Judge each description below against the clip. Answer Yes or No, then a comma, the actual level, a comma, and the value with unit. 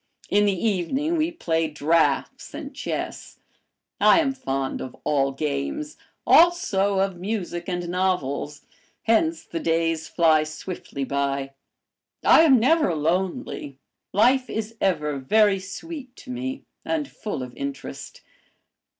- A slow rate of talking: Yes, slow, 125 wpm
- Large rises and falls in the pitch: Yes, wide, 8.9 semitones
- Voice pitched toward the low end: No, medium, 185 Hz